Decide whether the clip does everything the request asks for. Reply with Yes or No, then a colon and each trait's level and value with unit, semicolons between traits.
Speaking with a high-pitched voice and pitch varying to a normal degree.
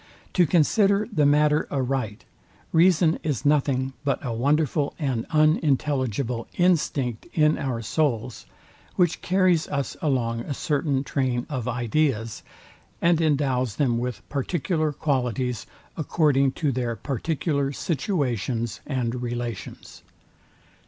No: medium, 140 Hz; average, 3.9 semitones